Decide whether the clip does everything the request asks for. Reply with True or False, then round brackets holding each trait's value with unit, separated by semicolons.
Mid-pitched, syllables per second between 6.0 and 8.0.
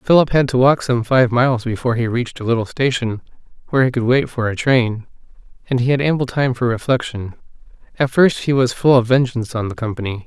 False (125 Hz; 6.1 syllables/s)